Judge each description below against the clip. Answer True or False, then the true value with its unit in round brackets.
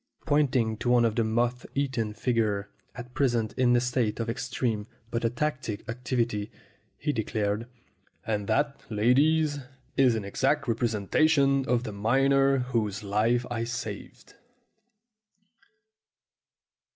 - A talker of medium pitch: False (120 Hz)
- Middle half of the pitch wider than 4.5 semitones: False (3.3 semitones)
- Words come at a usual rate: False (120 wpm)